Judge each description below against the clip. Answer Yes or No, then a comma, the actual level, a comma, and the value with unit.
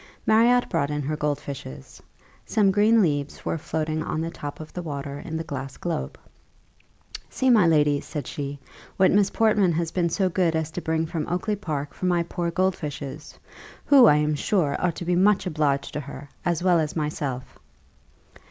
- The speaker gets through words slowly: No, average, 190 wpm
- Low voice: No, medium, 160 Hz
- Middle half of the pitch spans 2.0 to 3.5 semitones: No, average, 3.9 semitones